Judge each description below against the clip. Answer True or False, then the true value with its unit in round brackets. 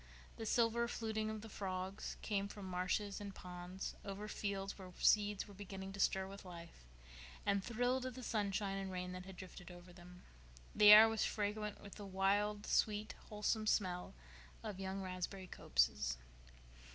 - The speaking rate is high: False (165 wpm)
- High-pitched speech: True (195 Hz)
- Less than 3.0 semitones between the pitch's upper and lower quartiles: True (2.4 semitones)